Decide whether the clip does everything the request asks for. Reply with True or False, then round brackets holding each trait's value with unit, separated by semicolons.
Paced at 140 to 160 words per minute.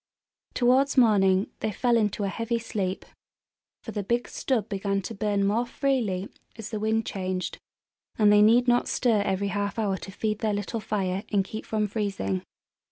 False (175 wpm)